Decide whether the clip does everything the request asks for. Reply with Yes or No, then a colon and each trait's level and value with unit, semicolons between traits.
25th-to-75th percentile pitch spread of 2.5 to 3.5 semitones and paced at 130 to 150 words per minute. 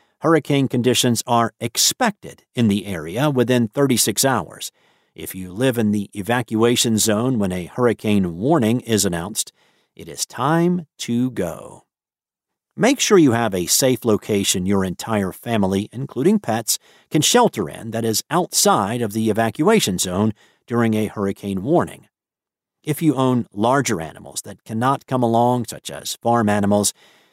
No: average, 4.0 semitones; average, 145 wpm